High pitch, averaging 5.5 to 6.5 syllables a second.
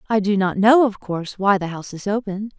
Yes: high, 205 Hz; 6.0 syllables/s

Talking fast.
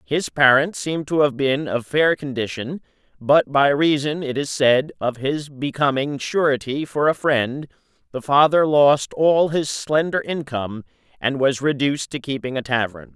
No: average, 165 wpm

